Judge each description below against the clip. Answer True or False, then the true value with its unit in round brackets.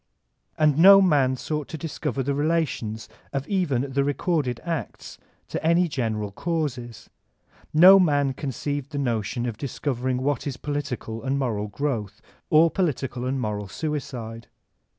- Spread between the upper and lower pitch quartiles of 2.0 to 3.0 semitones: False (4.1 semitones)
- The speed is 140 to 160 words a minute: True (145 wpm)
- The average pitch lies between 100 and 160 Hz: True (140 Hz)